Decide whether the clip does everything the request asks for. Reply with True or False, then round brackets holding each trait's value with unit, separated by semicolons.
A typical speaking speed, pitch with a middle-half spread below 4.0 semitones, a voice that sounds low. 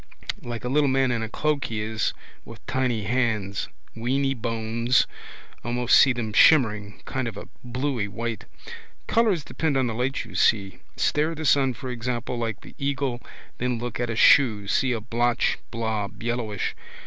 True (170 wpm; 2.9 semitones; 120 Hz)